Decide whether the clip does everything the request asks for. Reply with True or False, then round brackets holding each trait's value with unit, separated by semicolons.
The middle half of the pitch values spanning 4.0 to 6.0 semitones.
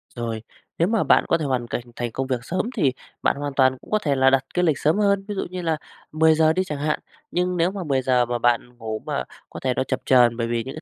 True (5.5 semitones)